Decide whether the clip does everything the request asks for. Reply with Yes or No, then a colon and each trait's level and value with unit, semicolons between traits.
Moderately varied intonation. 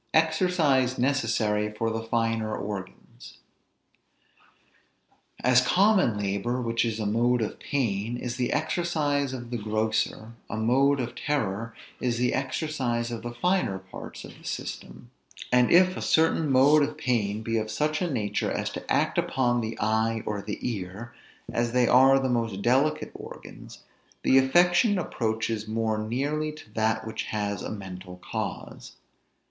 Yes: average, 3.9 semitones